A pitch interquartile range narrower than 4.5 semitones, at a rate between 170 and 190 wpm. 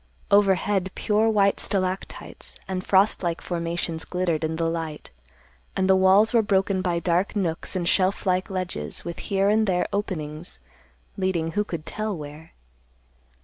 No: average, 2.8 semitones; average, 150 wpm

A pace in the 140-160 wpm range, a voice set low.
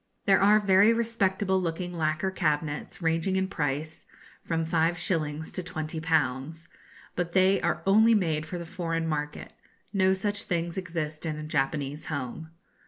No: average, 145 wpm; medium, 165 Hz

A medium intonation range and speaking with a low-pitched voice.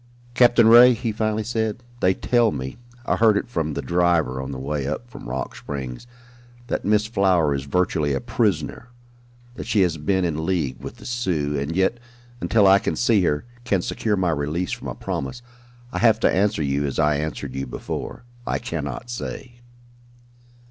No: wide, 7.5 semitones; very low, 90 Hz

